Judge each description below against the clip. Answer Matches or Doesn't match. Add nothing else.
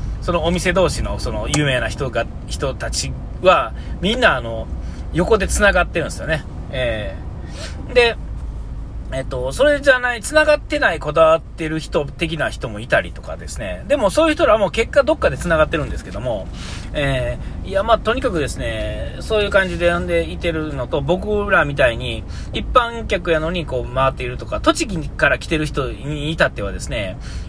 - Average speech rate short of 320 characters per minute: Doesn't match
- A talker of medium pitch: Matches